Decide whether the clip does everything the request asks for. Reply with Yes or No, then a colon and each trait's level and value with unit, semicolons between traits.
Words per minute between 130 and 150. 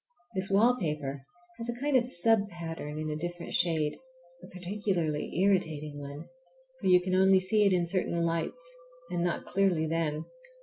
No: average, 165 wpm